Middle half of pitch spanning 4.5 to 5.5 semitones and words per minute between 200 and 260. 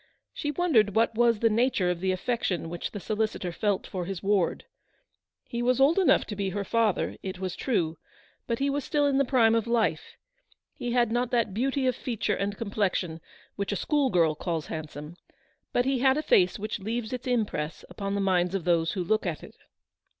Yes: average, 5.0 semitones; fast, 205 wpm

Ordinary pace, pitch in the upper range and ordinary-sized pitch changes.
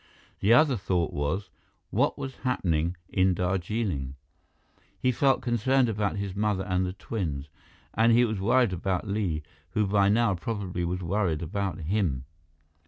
No: average, 150 wpm; low, 100 Hz; average, 3.8 semitones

